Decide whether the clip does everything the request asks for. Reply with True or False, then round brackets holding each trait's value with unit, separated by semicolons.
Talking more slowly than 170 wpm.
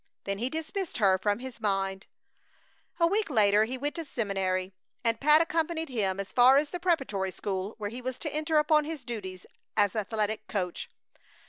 False (190 wpm)